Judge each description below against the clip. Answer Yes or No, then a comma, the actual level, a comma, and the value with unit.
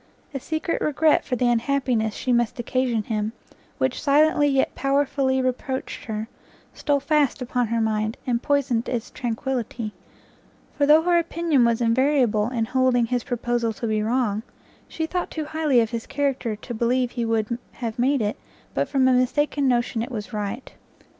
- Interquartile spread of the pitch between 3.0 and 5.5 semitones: Yes, average, 3.4 semitones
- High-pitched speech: Yes, very high, 250 Hz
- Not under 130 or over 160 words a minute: No, average, 170 wpm